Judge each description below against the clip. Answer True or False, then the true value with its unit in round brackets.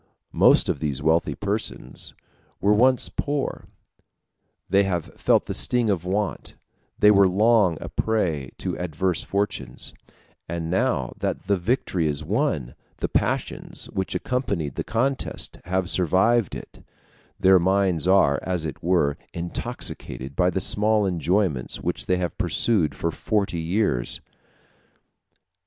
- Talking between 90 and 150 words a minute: True (135 wpm)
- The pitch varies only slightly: False (4.2 semitones)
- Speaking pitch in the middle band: False (95 Hz)